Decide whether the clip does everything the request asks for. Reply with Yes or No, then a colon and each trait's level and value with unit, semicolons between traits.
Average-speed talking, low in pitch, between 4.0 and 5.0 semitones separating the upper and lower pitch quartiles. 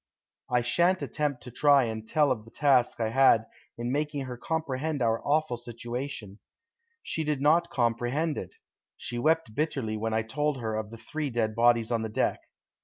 Yes: average, 180 wpm; low, 125 Hz; average, 4.5 semitones